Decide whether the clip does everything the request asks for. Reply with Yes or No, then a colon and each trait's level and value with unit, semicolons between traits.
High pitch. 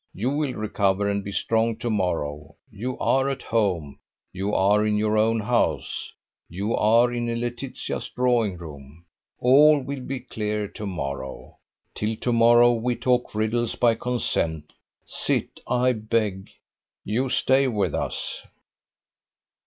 No: low, 110 Hz